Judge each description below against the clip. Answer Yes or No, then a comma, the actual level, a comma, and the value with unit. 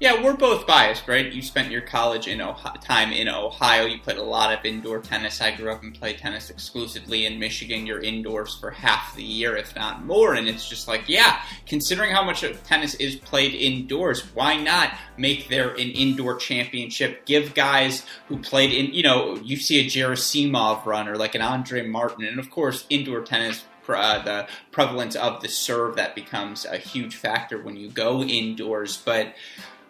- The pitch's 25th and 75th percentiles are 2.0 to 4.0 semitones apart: Yes, average, 3.7 semitones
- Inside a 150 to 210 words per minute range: Yes, average, 195 wpm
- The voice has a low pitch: Yes, low, 125 Hz